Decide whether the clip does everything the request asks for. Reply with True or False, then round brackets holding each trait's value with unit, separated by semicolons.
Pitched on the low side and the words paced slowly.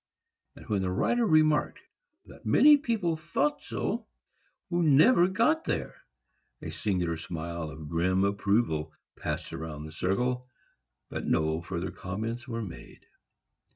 True (100 Hz; 130 wpm)